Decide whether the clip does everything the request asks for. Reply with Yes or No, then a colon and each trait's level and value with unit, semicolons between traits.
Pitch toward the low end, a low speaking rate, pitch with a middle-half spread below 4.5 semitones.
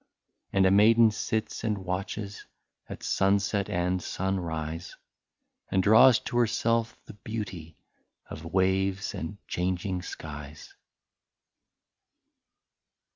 Yes: very low, 95 Hz; slow, 95 wpm; average, 3.1 semitones